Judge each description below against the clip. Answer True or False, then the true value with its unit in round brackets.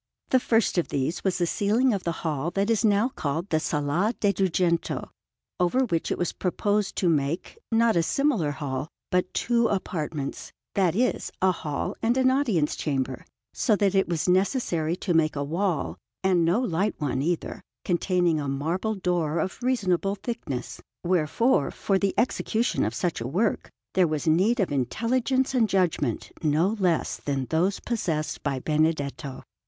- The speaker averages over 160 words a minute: True (170 wpm)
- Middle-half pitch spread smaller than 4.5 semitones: False (5.2 semitones)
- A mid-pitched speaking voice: True (180 Hz)